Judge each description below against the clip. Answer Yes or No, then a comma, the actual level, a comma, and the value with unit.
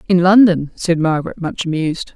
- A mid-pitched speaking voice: Yes, medium, 170 Hz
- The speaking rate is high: No, average, 165 wpm